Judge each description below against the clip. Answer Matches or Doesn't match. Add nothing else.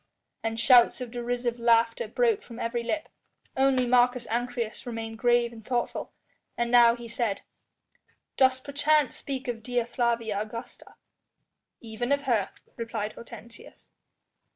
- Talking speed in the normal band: Doesn't match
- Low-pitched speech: Doesn't match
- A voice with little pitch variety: Matches